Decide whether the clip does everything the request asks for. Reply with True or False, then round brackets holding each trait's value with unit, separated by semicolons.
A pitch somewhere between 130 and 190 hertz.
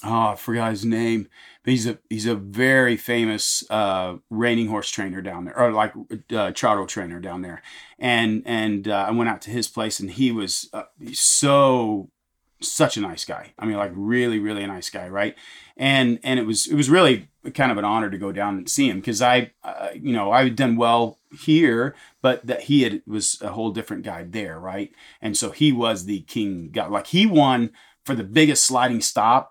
False (115 Hz)